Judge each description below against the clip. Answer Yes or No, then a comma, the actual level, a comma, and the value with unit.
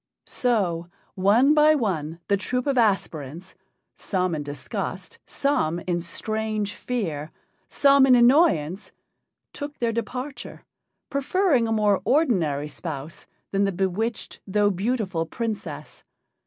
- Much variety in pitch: Yes, wide, 6.6 semitones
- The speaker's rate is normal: No, slow, 115 wpm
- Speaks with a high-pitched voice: Yes, high, 205 Hz